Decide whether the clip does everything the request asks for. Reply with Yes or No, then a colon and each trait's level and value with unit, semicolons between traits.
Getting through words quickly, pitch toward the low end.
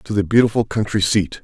Yes: fast, 210 wpm; low, 105 Hz